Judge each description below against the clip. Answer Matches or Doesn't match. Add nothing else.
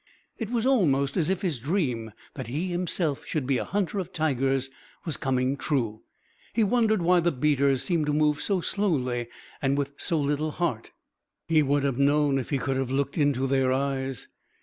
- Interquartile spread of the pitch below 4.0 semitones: Doesn't match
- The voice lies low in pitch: Doesn't match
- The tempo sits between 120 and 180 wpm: Doesn't match